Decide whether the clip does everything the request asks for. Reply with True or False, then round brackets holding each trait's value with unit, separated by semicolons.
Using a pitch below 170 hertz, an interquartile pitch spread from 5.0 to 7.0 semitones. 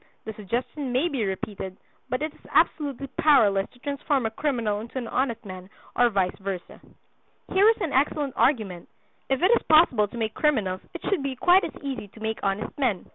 False (245 Hz; 5.5 semitones)